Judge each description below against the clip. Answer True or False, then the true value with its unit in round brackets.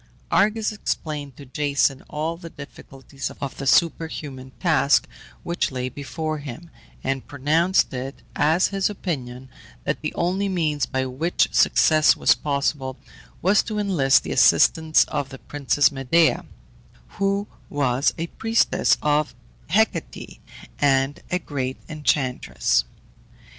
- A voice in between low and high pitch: True (145 Hz)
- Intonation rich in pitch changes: False (3.8 semitones)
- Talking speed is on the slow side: True (125 wpm)